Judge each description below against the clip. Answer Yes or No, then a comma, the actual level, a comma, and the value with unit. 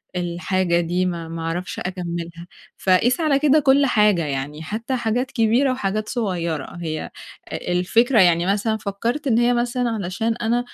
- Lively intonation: Yes, wide, 5.7 semitones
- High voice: Yes, high, 200 Hz